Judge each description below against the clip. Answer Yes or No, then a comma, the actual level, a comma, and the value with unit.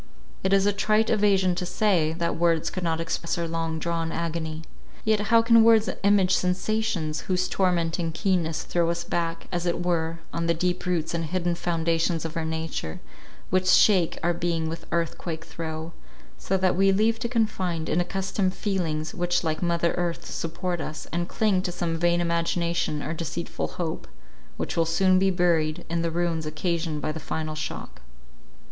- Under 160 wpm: No, average, 180 wpm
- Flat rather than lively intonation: Yes, narrow, 2.1 semitones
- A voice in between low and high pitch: Yes, medium, 170 Hz